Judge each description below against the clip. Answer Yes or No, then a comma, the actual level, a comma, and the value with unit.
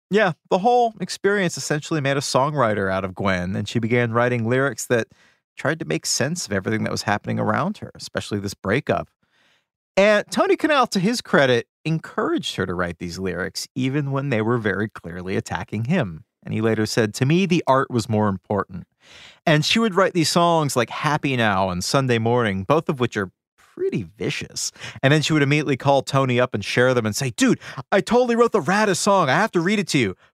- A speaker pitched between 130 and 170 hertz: Yes, low, 135 Hz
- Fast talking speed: Yes, fast, 210 wpm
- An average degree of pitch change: No, wide, 8.1 semitones